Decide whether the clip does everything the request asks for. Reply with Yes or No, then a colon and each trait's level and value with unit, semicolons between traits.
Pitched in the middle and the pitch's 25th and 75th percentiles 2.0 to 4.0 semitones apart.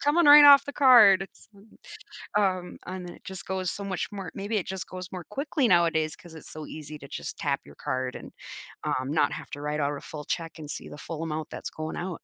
No: medium, 180 Hz; average, 4.5 semitones